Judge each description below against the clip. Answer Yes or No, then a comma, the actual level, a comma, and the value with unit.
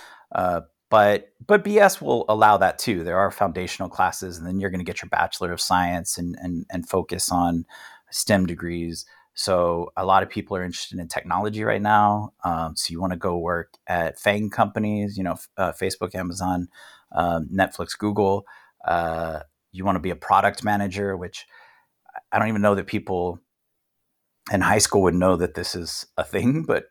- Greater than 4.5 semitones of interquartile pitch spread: No, average, 3.2 semitones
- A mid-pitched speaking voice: No, very low, 95 Hz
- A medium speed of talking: Yes, average, 185 wpm